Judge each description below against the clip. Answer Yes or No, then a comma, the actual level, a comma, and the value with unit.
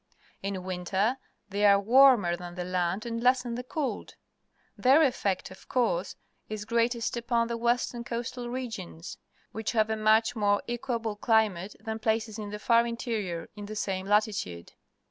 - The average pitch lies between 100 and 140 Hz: No, high, 220 Hz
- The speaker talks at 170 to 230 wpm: No, average, 160 wpm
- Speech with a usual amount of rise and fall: Yes, average, 3.1 semitones